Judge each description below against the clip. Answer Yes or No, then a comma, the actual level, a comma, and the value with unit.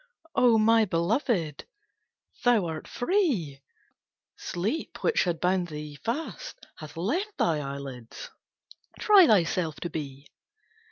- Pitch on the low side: No, medium, 180 Hz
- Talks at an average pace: No, slow, 110 wpm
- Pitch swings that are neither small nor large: No, wide, 7.7 semitones